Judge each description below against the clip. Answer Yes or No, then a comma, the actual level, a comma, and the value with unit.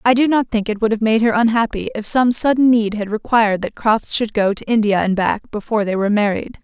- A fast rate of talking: Yes, fast, 255 wpm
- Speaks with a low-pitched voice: No, high, 220 Hz